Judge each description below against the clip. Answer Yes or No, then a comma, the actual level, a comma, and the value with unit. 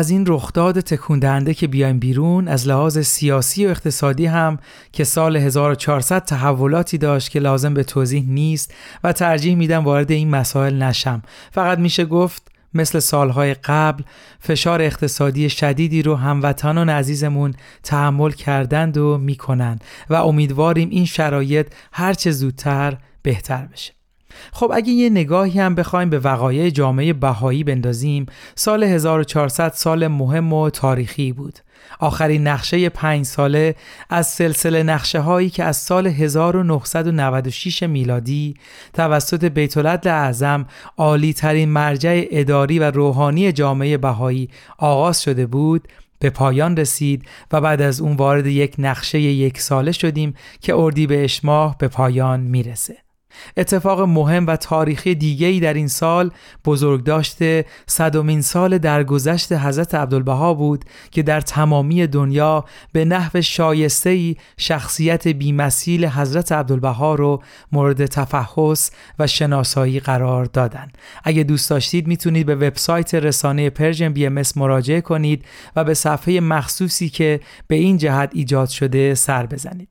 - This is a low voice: No, medium, 150 Hz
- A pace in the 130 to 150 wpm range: Yes, average, 135 wpm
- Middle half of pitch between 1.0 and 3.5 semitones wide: Yes, average, 2.8 semitones